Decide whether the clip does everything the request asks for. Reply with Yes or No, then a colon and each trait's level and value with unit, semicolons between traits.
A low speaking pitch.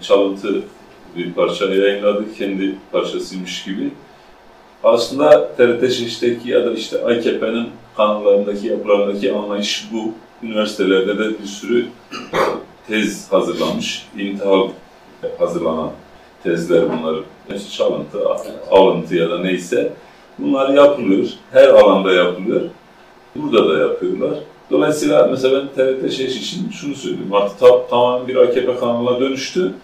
Yes: low, 110 Hz